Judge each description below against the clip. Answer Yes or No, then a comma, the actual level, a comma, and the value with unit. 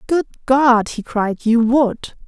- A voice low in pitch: No, high, 245 Hz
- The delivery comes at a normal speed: Yes, average, 160 wpm